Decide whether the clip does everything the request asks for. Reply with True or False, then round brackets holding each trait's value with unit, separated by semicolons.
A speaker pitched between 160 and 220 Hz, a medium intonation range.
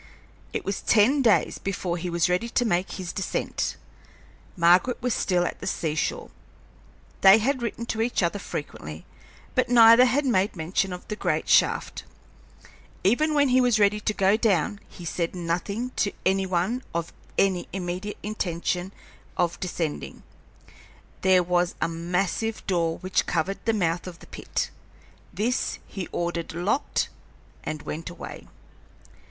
True (190 Hz; 4.2 semitones)